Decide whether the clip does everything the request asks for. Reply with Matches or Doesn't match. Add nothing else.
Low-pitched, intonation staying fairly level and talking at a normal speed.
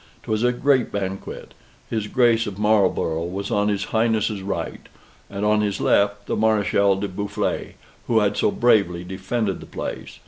Matches